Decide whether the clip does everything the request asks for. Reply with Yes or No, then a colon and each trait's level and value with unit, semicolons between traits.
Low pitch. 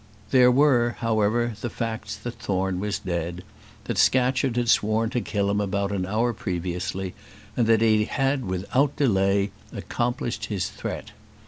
Yes: low, 110 Hz